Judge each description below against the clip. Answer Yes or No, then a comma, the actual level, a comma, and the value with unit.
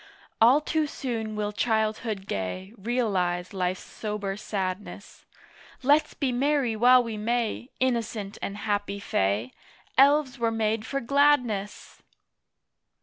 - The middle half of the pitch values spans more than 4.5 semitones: No, average, 3.8 semitones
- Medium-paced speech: No, slow, 115 wpm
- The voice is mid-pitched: No, high, 220 Hz